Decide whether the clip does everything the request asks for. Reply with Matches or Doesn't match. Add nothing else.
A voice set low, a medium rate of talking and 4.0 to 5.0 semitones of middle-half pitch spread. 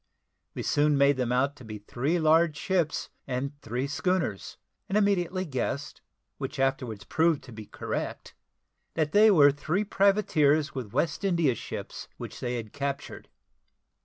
Doesn't match